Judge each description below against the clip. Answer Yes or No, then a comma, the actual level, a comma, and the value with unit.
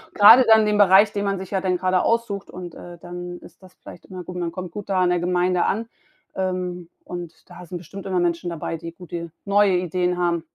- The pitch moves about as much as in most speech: No, narrow, 1.8 semitones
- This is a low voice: No, medium, 180 Hz